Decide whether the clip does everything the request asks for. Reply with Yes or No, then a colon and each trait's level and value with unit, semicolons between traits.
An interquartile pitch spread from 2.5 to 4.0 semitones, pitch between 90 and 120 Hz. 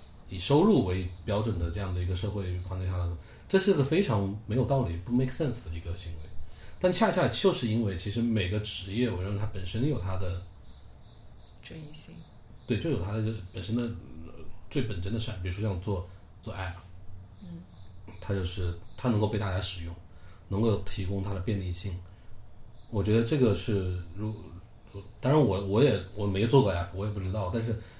Yes: average, 3.7 semitones; low, 100 Hz